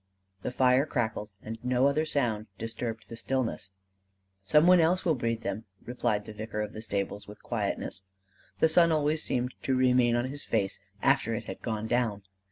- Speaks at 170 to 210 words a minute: Yes, average, 180 wpm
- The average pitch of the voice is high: No, low, 120 Hz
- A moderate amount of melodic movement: Yes, average, 3.8 semitones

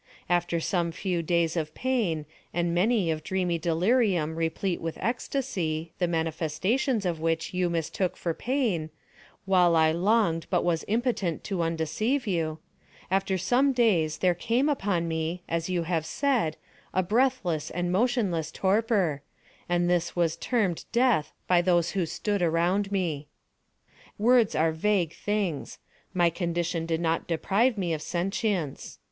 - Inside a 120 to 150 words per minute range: Yes, average, 140 wpm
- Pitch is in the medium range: Yes, medium, 175 Hz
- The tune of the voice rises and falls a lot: No, average, 4.0 semitones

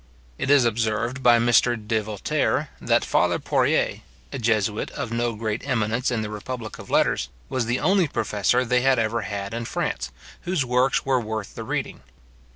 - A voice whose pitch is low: Yes, low, 115 Hz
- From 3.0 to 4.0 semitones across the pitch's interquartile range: No, narrow, 2.5 semitones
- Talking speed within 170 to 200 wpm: Yes, average, 175 wpm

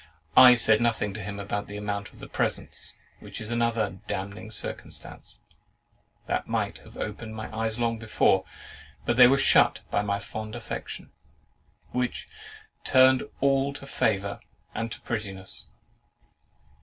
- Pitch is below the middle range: Yes, low, 110 Hz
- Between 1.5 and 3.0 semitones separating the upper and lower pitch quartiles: Yes, average, 2.7 semitones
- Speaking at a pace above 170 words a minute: No, average, 145 wpm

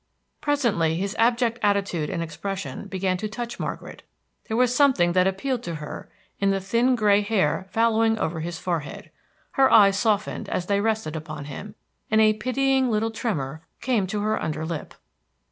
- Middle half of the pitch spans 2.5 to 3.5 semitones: No, average, 4.7 semitones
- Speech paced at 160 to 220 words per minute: Yes, average, 170 wpm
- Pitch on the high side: Yes, high, 205 Hz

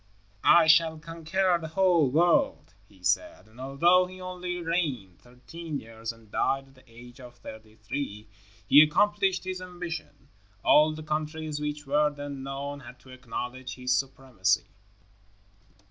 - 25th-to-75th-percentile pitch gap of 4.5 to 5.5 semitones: Yes, average, 5.1 semitones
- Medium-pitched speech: Yes, medium, 145 Hz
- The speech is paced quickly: No, average, 145 wpm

